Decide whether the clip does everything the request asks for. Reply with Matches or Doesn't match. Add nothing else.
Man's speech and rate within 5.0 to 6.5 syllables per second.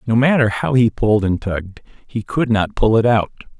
Matches